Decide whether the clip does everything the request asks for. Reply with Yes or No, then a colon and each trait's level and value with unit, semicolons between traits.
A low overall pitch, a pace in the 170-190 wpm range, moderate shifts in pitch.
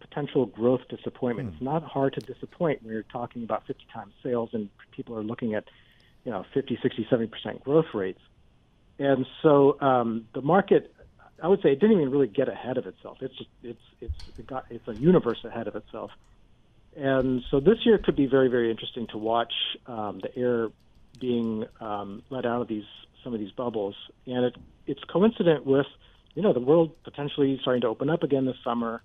No: low, 125 Hz; average, 200 wpm; average, 3.3 semitones